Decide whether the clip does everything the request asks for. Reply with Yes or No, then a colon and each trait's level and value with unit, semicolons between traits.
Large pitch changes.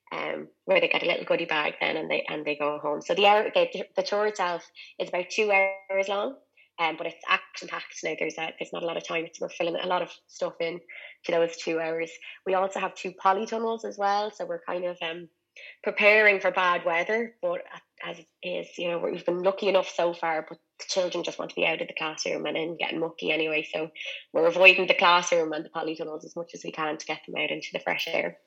No: average, 2.8 semitones